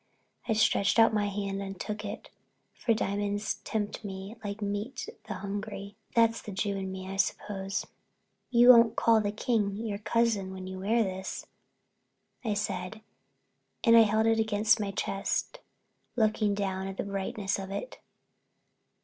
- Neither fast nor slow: Yes, average, 155 wpm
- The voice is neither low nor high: No, high, 205 Hz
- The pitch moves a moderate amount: No, narrow, 2.0 semitones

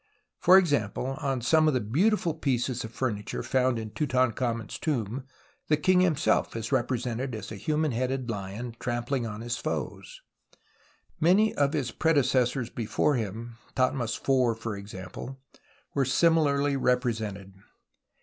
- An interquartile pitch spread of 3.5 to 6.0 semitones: Yes, average, 3.8 semitones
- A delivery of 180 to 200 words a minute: No, average, 145 wpm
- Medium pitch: No, low, 125 Hz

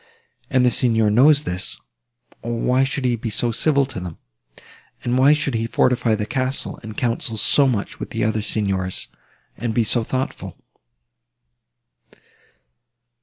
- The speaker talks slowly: No, average, 150 wpm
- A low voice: Yes, low, 120 Hz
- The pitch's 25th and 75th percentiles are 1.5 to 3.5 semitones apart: Yes, average, 3.0 semitones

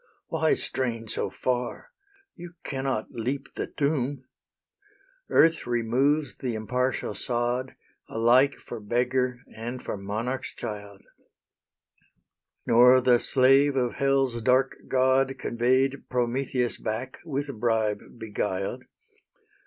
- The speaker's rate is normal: No, slow, 105 wpm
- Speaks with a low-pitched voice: Yes, low, 125 Hz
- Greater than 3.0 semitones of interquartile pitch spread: No, narrow, 2.4 semitones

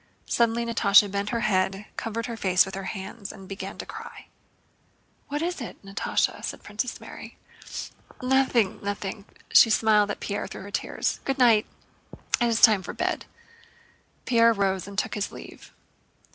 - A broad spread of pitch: No, average, 2.9 semitones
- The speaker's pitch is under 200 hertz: No, high, 210 Hz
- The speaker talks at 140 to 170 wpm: Yes, average, 160 wpm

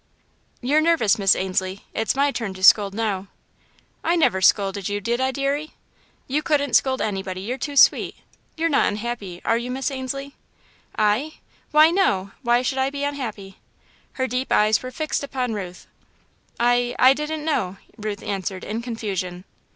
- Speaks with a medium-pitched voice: No, high, 240 Hz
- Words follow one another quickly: No, average, 165 wpm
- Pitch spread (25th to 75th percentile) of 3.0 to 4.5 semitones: No, wide, 5.6 semitones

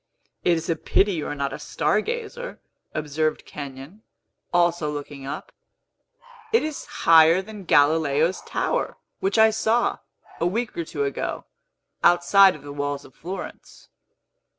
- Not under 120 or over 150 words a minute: Yes, average, 145 wpm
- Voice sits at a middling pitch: Yes, medium, 165 Hz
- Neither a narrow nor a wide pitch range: No, wide, 6.2 semitones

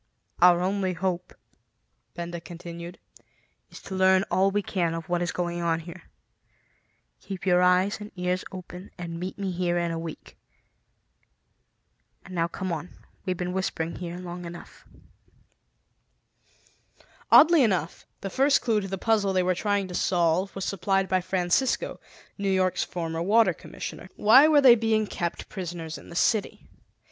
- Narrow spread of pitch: Yes, narrow, 2.1 semitones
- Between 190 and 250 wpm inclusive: No, average, 155 wpm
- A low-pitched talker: No, medium, 180 Hz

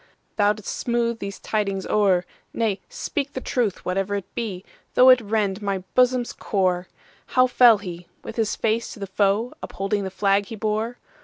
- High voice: Yes, high, 210 Hz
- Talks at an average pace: Yes, average, 150 wpm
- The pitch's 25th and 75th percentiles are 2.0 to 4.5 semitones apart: Yes, average, 3.1 semitones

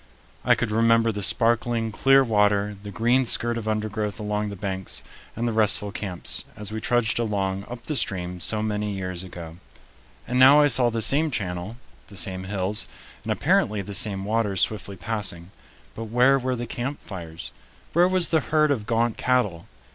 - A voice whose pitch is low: Yes, low, 110 Hz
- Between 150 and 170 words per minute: No, average, 180 wpm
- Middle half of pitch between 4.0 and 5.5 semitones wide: No, average, 3.2 semitones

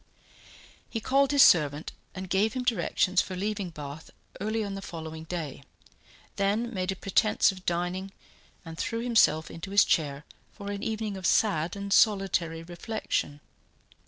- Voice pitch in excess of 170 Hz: Yes, high, 190 Hz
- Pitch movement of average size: Yes, average, 4.4 semitones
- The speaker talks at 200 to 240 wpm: No, average, 155 wpm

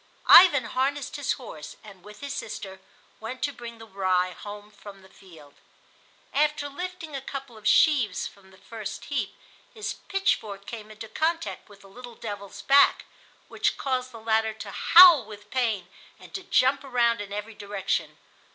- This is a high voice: Yes, high, 225 Hz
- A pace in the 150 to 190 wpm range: Yes, average, 170 wpm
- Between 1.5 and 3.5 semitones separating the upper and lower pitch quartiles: No, average, 5.2 semitones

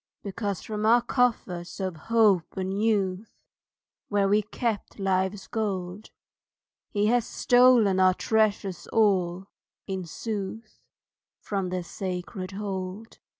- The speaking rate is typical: No, slow, 110 wpm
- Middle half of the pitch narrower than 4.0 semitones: Yes, average, 2.8 semitones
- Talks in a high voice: Yes, high, 200 Hz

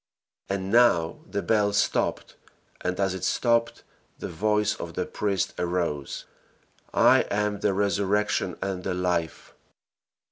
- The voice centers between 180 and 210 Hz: No, low, 100 Hz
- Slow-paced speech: Yes, slow, 130 wpm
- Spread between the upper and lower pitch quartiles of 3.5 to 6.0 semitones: No, narrow, 2.4 semitones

